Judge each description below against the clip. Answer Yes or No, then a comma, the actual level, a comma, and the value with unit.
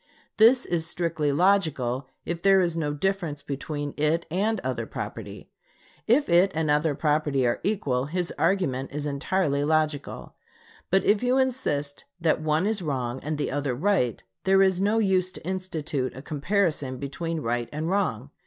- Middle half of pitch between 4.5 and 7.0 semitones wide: Yes, average, 5.0 semitones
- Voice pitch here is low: No, medium, 160 Hz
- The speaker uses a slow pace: No, average, 160 wpm